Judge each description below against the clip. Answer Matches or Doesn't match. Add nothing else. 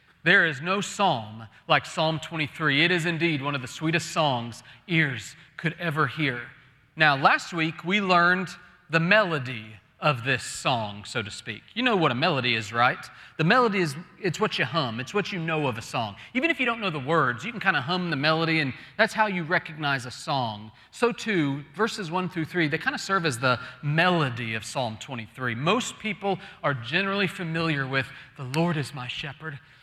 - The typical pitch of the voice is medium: Matches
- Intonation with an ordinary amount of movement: Doesn't match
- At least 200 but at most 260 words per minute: Matches